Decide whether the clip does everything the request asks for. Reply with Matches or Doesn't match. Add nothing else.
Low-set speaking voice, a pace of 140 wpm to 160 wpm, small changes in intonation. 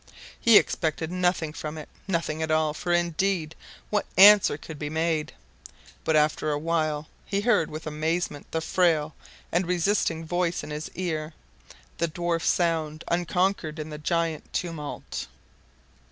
Doesn't match